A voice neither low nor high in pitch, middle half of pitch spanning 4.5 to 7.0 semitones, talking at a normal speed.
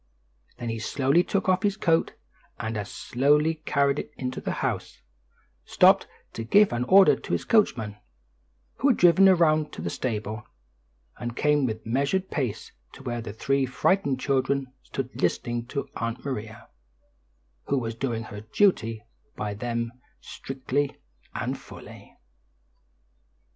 No: low, 130 Hz; average, 4.9 semitones; average, 145 wpm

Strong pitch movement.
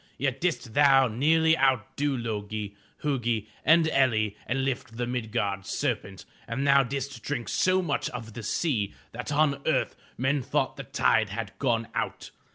No: average, 3.8 semitones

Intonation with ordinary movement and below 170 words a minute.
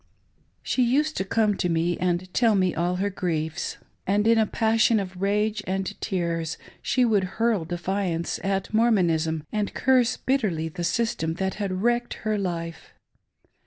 Yes: average, 4.1 semitones; average, 160 wpm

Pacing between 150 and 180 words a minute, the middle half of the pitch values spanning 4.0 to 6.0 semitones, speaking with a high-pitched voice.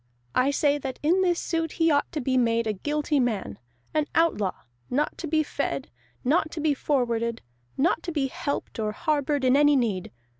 No: average, 190 wpm; average, 4.4 semitones; very high, 285 Hz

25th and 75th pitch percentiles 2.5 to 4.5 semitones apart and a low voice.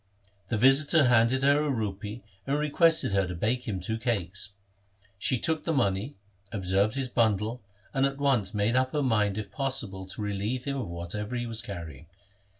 No: average, 5.2 semitones; low, 115 Hz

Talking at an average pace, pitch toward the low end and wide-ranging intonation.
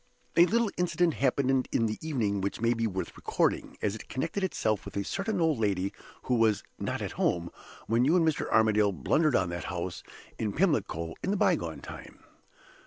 Yes: average, 190 wpm; low, 115 Hz; wide, 8.1 semitones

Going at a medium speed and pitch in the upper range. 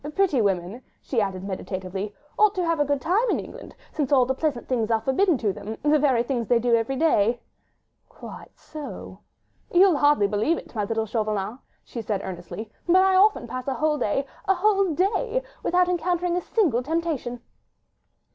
Yes: average, 170 wpm; very high, 265 Hz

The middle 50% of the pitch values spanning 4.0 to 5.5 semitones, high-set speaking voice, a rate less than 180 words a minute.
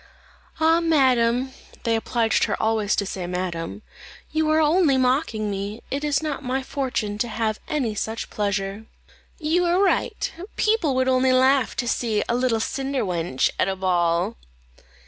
Yes: average, 5.2 semitones; high, 240 Hz; average, 160 wpm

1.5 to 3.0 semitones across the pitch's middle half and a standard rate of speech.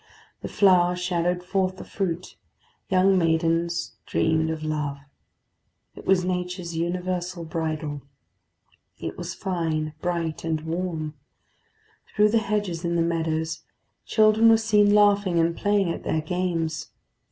No: narrow, 2.5 semitones; slow, 130 wpm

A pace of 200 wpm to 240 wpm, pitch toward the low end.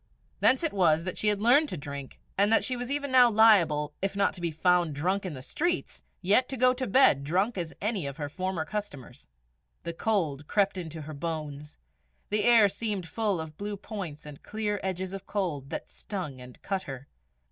No: fast, 205 wpm; medium, 185 Hz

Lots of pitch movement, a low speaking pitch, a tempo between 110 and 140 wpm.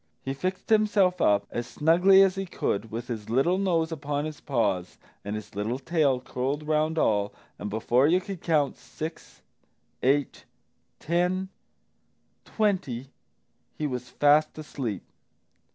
No: wide, 6.3 semitones; medium, 145 Hz; slow, 135 wpm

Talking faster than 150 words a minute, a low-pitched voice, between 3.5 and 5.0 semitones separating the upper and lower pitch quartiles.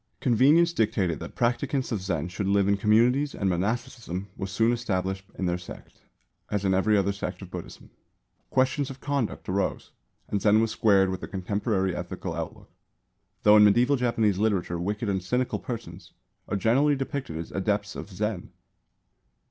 Yes: average, 165 wpm; low, 100 Hz; average, 4.0 semitones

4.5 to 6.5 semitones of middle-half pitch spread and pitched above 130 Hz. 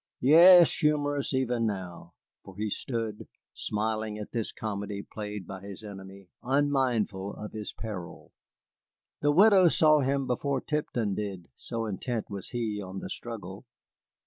No: average, 5.1 semitones; low, 110 Hz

